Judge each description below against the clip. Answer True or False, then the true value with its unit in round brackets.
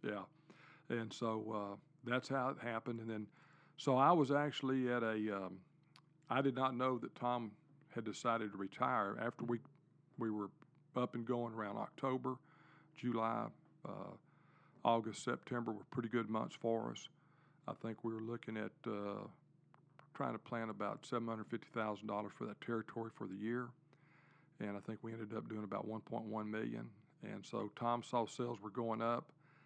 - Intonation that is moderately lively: True (3.8 semitones)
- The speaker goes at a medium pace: True (180 wpm)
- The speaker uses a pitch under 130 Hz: True (120 Hz)